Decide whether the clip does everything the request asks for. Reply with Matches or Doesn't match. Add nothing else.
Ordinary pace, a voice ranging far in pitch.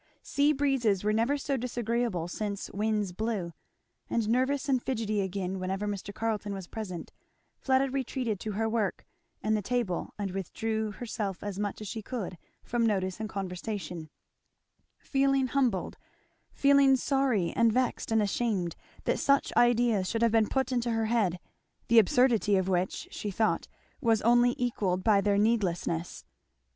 Doesn't match